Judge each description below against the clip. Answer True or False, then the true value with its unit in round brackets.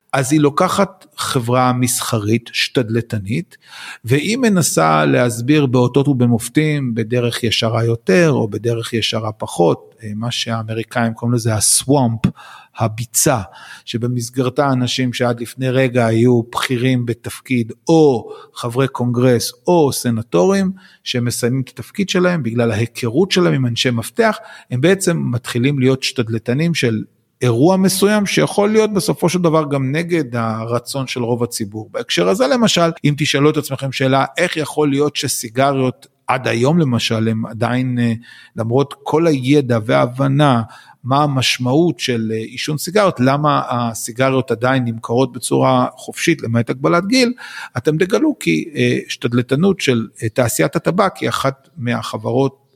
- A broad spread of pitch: False (4.2 semitones)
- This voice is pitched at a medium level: False (125 Hz)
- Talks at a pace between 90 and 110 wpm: False (125 wpm)